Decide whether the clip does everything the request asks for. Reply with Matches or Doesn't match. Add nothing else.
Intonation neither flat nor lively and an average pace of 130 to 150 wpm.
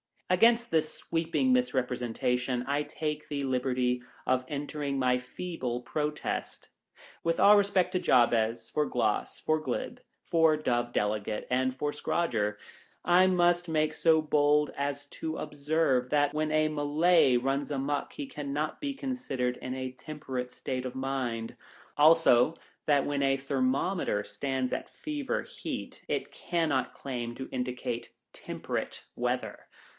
Matches